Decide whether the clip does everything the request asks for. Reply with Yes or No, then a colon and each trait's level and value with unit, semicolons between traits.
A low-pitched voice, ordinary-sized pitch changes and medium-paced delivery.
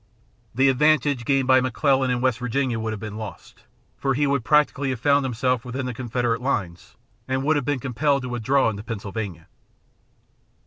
Yes: low, 130 Hz; average, 3.2 semitones; average, 180 wpm